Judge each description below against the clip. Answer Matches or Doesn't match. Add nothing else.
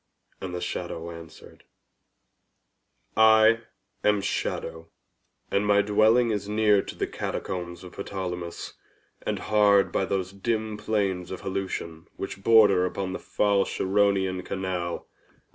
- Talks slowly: Matches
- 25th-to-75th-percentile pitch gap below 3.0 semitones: Matches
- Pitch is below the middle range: Matches